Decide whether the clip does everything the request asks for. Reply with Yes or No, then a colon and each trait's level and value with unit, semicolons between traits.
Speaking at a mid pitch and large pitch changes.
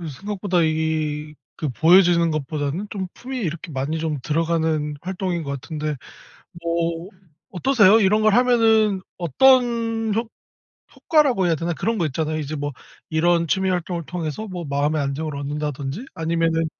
No: medium, 170 Hz; average, 4.4 semitones